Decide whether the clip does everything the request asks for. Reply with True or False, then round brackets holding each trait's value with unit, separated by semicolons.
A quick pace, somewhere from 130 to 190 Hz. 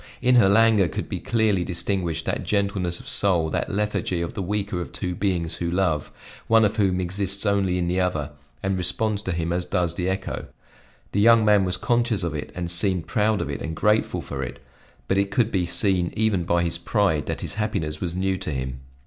False (215 wpm; 95 Hz)